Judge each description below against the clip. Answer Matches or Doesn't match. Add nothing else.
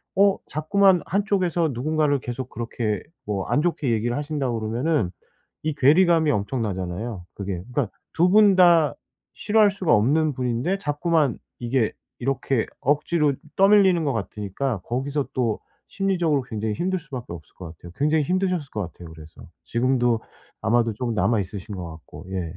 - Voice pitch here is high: Doesn't match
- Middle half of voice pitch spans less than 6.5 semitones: Doesn't match